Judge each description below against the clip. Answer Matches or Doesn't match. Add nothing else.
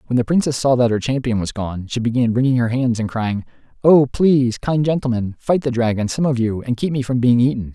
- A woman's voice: Doesn't match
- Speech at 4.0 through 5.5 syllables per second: Doesn't match